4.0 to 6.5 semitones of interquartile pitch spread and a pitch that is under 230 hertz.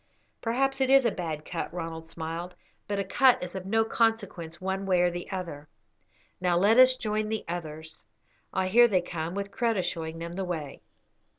Yes: average, 4.7 semitones; medium, 185 Hz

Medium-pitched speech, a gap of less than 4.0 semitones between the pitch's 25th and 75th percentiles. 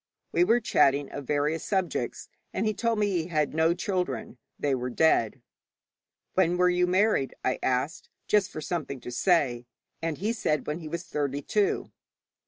No: medium, 160 Hz; average, 4.8 semitones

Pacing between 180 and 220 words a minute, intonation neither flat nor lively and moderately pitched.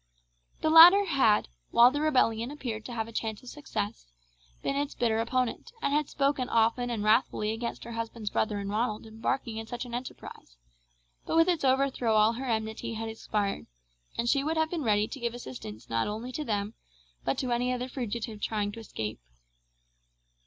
No: average, 190 wpm; average, 3.4 semitones; high, 235 Hz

